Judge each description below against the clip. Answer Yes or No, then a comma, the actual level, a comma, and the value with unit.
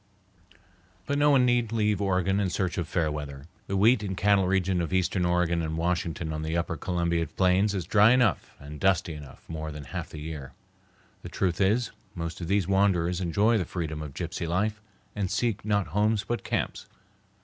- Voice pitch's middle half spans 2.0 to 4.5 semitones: Yes, average, 3.7 semitones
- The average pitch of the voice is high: No, very low, 90 Hz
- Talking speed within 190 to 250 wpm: Yes, average, 195 wpm